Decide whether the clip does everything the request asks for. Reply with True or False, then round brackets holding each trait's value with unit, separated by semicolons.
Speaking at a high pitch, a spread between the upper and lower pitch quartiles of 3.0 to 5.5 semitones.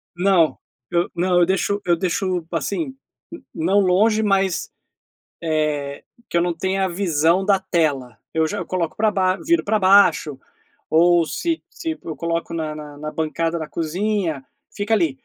False (175 Hz; 3.6 semitones)